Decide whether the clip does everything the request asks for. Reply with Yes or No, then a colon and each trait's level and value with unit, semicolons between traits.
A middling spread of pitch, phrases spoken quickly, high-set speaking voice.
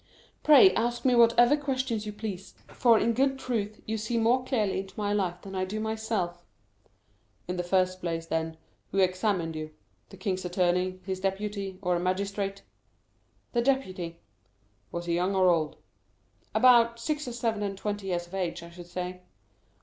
No: average, 4.1 semitones; average, 170 wpm; high, 195 Hz